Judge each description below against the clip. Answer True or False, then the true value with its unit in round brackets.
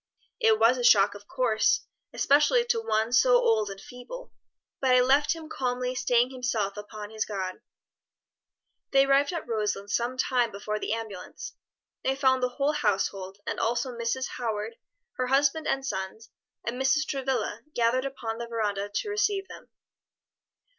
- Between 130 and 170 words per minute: True (160 wpm)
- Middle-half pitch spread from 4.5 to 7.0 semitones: False (3.8 semitones)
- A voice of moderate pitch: False (245 Hz)